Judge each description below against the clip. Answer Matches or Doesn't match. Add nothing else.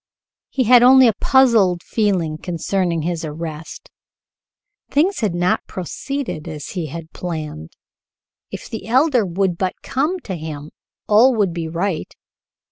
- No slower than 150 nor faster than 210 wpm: Doesn't match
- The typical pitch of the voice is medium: Matches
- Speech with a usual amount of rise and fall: Doesn't match